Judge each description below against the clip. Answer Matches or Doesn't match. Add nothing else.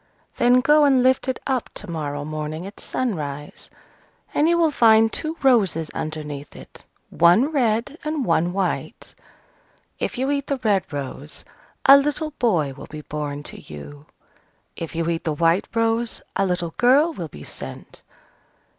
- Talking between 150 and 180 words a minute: Matches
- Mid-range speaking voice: Doesn't match